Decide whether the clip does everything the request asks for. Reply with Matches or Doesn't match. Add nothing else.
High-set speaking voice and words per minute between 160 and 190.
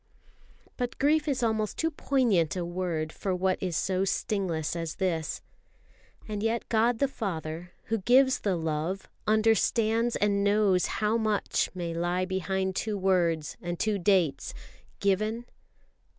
Doesn't match